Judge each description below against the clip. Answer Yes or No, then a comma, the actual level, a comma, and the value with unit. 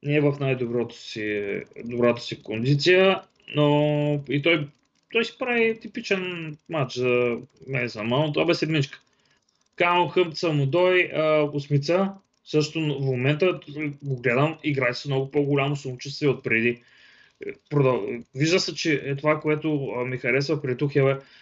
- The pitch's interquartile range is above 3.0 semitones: Yes, average, 4.2 semitones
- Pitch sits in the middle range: Yes, medium, 145 Hz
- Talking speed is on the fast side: No, average, 135 wpm